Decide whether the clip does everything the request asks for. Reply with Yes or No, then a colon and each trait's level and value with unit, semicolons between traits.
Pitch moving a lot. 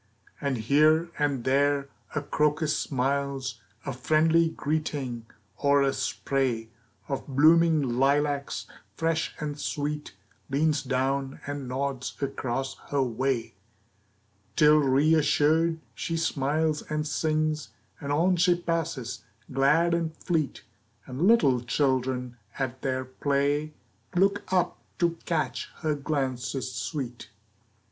No: average, 2.8 semitones